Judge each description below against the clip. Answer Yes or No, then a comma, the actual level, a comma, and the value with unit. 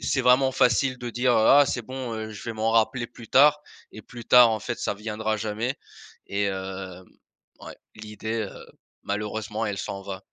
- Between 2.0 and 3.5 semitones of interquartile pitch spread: Yes, average, 2.9 semitones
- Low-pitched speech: Yes, low, 110 Hz